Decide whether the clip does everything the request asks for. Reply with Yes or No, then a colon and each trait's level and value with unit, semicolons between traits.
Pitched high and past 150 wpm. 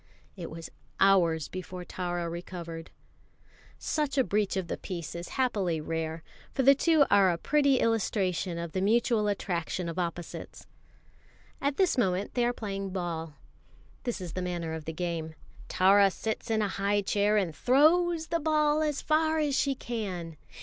Yes: high, 195 Hz; average, 165 wpm